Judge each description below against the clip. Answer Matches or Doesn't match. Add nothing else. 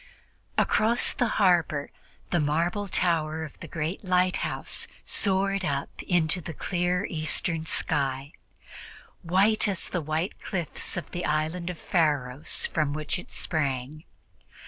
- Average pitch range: Matches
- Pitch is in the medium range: Matches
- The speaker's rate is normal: Doesn't match